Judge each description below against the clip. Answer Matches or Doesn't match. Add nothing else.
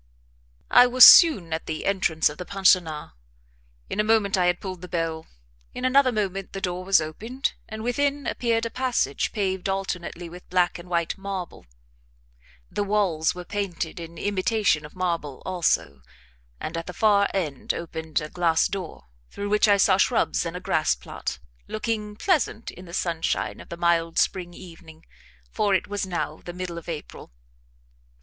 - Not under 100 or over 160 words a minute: Doesn't match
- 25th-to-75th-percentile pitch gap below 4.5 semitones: Matches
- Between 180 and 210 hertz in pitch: Matches